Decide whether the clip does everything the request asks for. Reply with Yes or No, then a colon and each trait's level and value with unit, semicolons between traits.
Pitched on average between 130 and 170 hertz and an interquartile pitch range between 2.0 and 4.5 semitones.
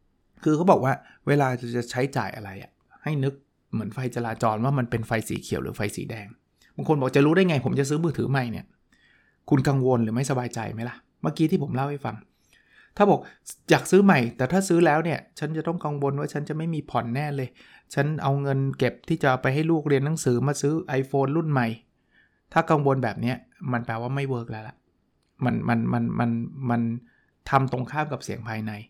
Yes: low, 135 Hz; average, 4.0 semitones